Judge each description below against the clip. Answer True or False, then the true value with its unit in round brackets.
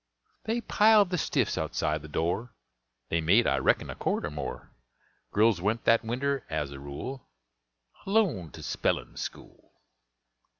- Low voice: True (110 Hz)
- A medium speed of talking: True (145 wpm)